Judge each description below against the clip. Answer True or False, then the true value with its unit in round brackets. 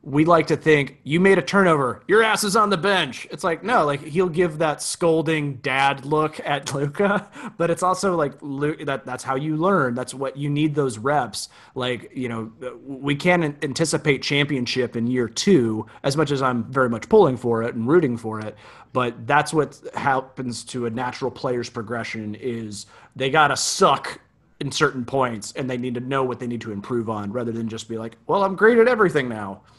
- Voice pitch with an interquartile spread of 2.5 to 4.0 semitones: False (4.6 semitones)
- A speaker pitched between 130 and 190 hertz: True (135 Hz)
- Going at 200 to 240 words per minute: True (205 wpm)